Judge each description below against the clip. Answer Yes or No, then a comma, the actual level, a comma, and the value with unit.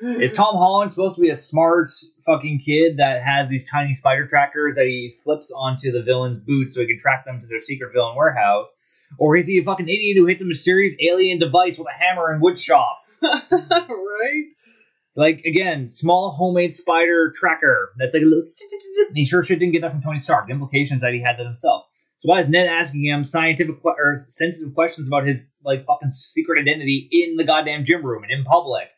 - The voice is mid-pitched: Yes, medium, 160 Hz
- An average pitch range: Yes, average, 4.3 semitones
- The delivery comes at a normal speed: No, fast, 210 wpm